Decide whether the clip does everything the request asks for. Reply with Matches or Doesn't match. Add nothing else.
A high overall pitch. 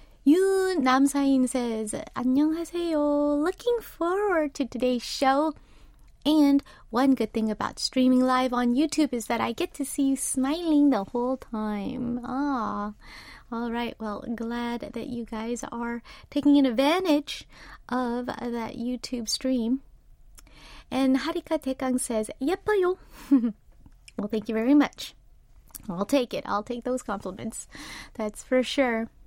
Matches